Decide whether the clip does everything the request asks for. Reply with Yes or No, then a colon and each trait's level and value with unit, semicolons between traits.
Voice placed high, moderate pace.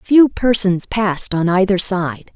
Yes: high, 195 Hz; average, 155 wpm